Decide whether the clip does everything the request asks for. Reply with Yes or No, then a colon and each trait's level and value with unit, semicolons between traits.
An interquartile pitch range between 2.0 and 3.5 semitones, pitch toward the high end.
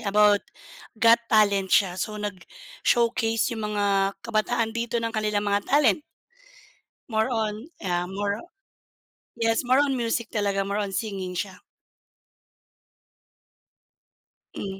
Yes: narrow, 2.4 semitones; high, 210 Hz